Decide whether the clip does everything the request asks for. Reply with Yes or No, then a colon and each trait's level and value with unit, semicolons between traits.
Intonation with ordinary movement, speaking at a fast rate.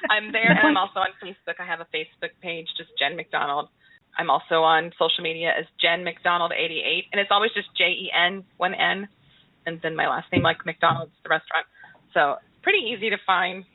Yes: average, 3.3 semitones; fast, 210 wpm